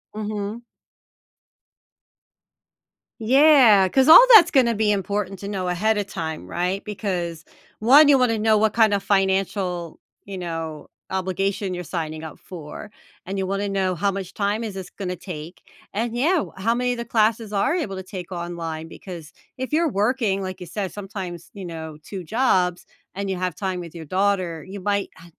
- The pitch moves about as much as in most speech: Yes, average, 3.3 semitones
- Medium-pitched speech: No, high, 195 Hz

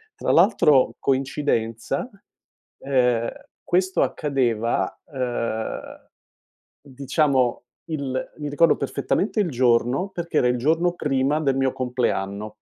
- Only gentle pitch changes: No, average, 3.7 semitones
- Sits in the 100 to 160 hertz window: Yes, low, 135 Hz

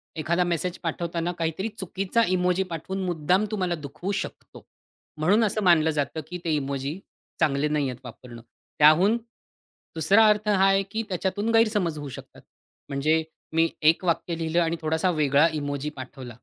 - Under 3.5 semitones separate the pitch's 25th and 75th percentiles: No, average, 3.9 semitones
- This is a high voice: No, medium, 165 Hz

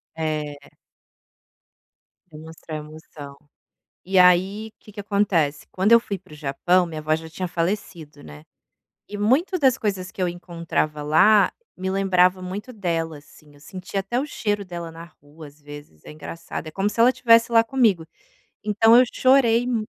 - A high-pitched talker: No, medium, 180 Hz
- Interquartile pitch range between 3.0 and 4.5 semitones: No, average, 5.0 semitones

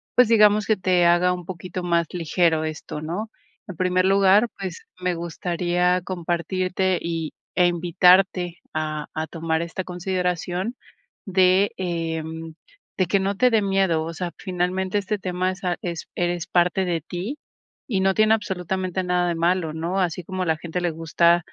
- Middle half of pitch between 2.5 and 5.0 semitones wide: No, narrow, 1.9 semitones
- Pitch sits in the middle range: Yes, medium, 180 Hz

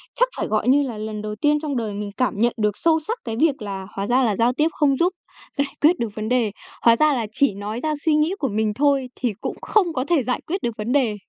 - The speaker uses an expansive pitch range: Yes, wide, 5.7 semitones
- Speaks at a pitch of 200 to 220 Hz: No, very high, 250 Hz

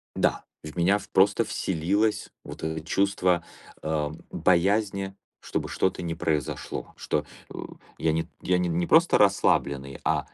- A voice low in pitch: Yes, very low, 90 Hz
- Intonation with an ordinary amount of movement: Yes, average, 3.7 semitones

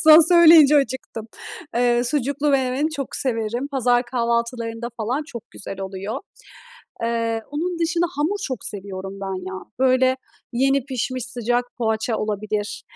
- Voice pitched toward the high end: Yes, high, 245 Hz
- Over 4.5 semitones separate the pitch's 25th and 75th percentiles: No, average, 3.7 semitones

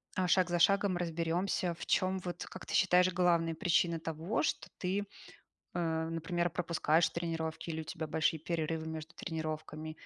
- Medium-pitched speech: Yes, medium, 170 Hz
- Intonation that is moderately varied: No, narrow, 1.9 semitones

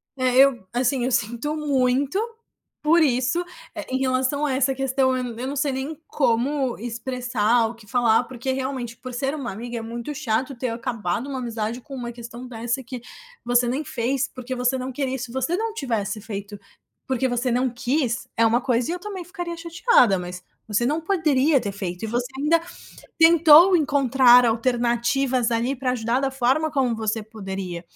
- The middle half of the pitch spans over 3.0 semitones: No, average, 2.7 semitones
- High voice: Yes, very high, 255 Hz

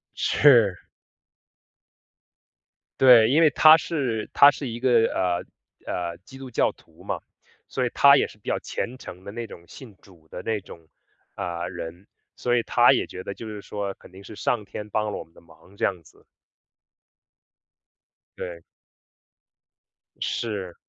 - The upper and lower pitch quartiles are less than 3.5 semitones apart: No, average, 5.3 semitones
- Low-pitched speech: Yes, low, 105 Hz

